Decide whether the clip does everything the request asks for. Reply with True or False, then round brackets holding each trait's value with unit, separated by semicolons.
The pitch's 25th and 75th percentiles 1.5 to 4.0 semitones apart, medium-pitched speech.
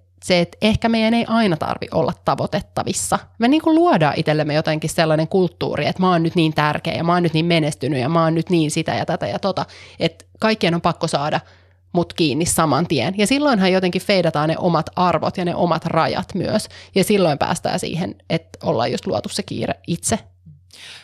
True (2.7 semitones; 165 Hz)